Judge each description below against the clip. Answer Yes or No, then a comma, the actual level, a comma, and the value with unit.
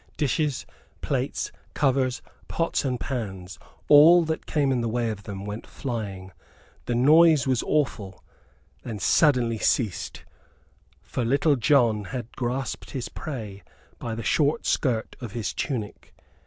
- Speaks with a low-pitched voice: Yes, low, 125 Hz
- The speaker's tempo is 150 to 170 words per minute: No, slow, 135 wpm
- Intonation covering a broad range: No, average, 4.4 semitones